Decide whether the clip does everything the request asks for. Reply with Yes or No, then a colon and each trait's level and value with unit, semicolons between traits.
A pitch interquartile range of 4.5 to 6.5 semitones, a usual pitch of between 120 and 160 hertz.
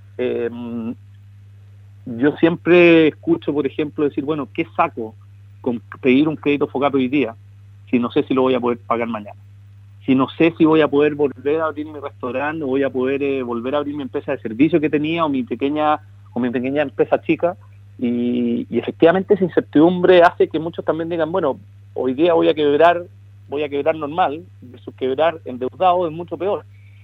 Yes: average, 5.1 semitones; medium, 140 Hz